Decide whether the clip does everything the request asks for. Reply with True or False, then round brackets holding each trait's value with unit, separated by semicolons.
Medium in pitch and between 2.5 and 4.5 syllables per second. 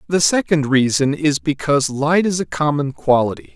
False (145 Hz; 5.0 syllables/s)